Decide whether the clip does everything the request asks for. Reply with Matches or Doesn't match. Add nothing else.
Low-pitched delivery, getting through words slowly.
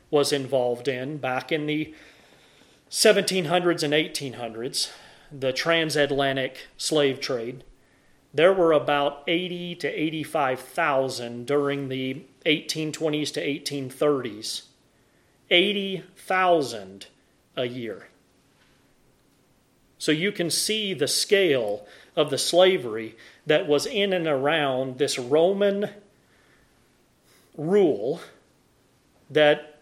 Doesn't match